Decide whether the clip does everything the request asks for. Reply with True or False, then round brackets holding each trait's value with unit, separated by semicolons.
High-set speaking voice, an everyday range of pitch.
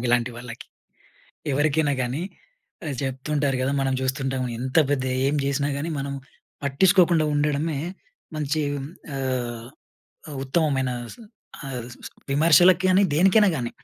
False (140 Hz; 3.0 semitones)